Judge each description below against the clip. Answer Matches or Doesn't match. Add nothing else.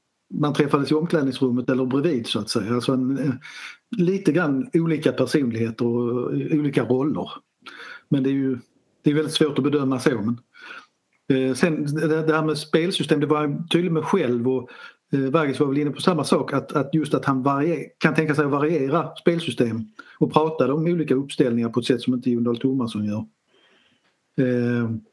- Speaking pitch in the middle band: Matches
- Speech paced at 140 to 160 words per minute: Doesn't match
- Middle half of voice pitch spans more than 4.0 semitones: Doesn't match